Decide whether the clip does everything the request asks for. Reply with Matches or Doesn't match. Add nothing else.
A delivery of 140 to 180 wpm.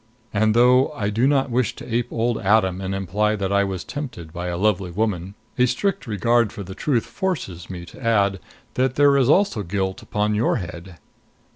Doesn't match